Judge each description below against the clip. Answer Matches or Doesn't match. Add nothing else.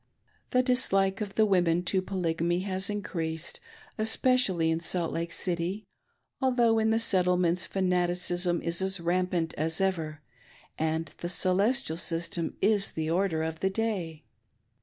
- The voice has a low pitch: Doesn't match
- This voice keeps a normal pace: Matches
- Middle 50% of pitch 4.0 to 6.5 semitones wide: Doesn't match